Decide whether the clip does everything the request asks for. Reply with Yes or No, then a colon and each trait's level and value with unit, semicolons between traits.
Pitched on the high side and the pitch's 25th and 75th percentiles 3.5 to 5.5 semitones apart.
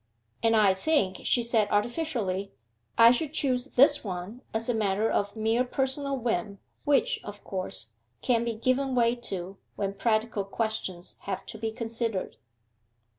Yes: high, 225 Hz; average, 3.8 semitones